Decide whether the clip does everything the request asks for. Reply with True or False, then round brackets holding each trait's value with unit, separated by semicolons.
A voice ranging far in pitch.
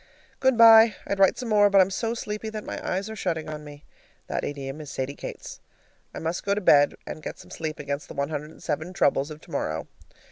True (6.2 semitones)